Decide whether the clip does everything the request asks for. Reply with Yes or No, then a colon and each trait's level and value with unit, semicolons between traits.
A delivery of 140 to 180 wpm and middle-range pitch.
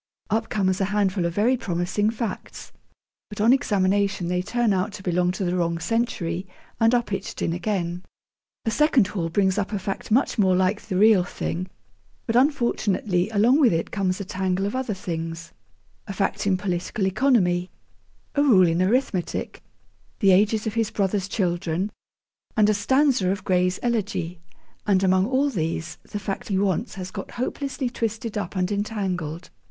No: average, 170 wpm; high, 195 Hz